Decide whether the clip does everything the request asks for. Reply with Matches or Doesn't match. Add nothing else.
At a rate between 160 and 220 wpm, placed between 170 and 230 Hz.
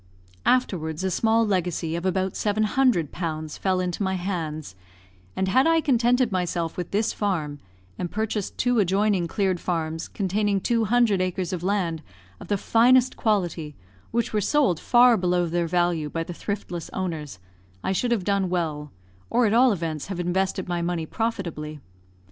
Matches